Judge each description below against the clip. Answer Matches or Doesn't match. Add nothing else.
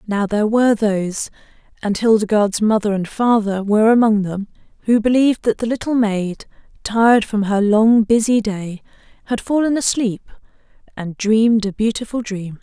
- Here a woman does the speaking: Matches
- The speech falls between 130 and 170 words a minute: Matches